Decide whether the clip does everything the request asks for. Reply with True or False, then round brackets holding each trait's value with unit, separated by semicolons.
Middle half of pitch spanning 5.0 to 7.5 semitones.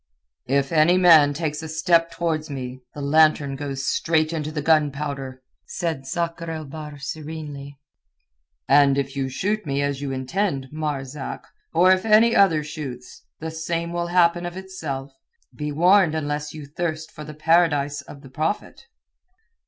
False (3.0 semitones)